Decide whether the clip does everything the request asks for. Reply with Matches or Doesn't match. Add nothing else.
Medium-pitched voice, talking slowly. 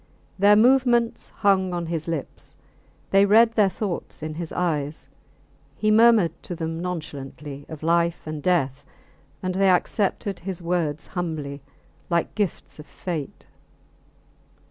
Matches